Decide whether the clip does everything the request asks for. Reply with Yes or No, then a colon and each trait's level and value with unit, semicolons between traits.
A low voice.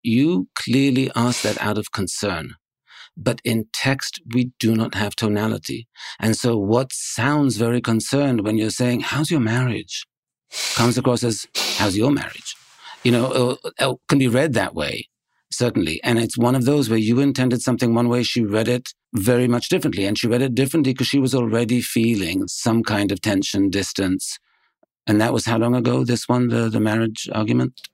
Yes: low, 120 Hz